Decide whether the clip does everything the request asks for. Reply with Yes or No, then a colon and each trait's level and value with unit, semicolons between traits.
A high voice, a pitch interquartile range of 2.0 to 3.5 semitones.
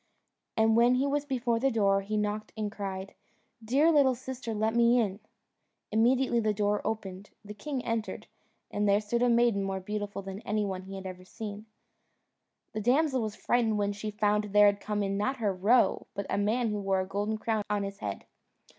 Yes: high, 210 Hz; average, 2.8 semitones